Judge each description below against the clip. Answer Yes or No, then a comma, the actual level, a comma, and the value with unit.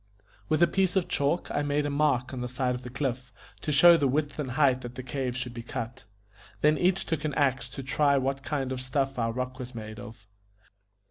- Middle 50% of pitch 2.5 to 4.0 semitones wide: Yes, average, 2.8 semitones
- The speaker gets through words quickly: Yes, fast, 230 wpm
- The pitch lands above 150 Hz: No, low, 135 Hz